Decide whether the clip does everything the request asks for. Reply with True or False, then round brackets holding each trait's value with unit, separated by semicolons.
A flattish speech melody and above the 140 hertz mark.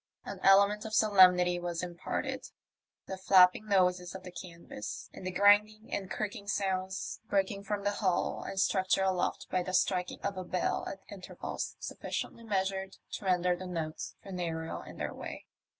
True (1.8 semitones; 190 Hz)